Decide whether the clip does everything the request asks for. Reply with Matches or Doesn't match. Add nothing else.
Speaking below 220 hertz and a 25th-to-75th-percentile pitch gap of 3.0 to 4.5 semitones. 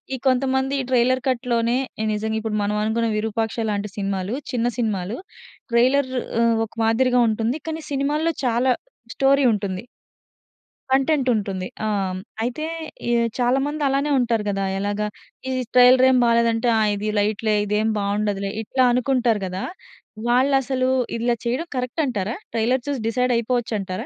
Doesn't match